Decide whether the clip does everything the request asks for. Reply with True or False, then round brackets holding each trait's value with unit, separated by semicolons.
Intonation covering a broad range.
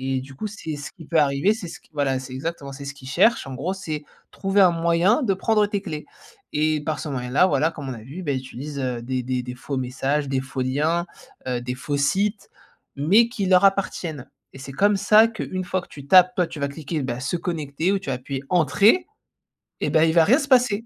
True (5.7 semitones)